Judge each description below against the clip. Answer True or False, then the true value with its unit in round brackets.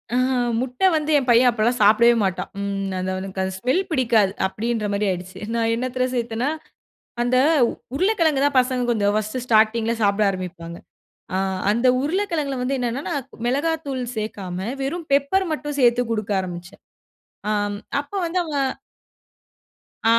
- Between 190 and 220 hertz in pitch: False (235 Hz)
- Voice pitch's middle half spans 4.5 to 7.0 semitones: True (5.0 semitones)